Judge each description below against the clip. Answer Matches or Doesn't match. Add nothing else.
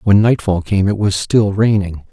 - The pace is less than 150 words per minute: Doesn't match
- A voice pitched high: Doesn't match